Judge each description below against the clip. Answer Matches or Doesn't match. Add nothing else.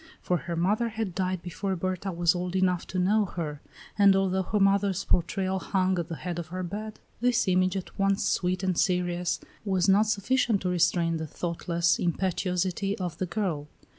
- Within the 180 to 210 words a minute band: Matches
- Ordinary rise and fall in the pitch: Doesn't match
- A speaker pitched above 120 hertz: Matches